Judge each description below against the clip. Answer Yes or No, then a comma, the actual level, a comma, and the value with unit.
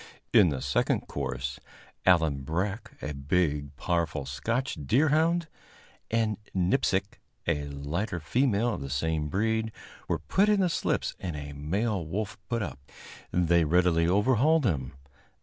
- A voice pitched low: Yes, very low, 90 Hz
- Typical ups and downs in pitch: No, wide, 7.2 semitones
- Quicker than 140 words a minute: No, slow, 135 wpm